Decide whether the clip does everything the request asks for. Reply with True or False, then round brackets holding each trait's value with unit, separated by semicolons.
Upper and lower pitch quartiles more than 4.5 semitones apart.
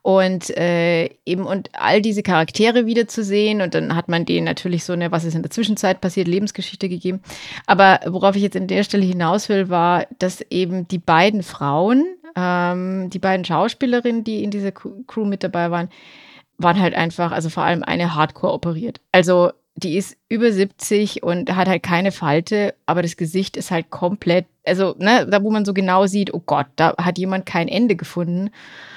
False (2.9 semitones)